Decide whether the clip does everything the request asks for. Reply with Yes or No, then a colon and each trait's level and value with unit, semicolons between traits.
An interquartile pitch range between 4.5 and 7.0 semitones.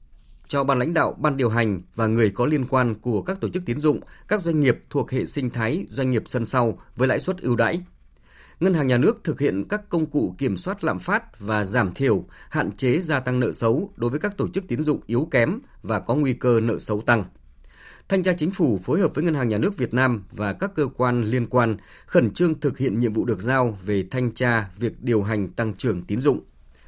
Yes: average, 4.9 semitones